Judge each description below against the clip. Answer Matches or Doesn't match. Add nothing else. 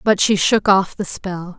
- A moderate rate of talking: Doesn't match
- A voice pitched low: Doesn't match